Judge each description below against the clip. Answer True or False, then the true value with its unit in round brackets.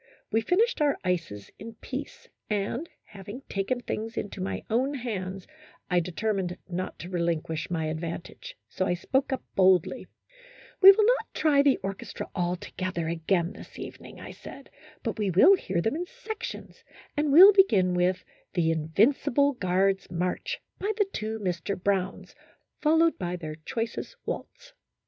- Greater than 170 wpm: False (165 wpm)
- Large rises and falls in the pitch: True (7.9 semitones)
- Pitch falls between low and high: False (195 Hz)